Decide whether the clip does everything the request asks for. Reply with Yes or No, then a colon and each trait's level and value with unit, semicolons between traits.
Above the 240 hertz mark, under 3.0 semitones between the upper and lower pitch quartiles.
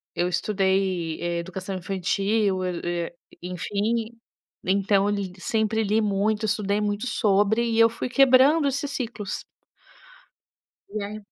No: high, 205 Hz; narrow, 2.6 semitones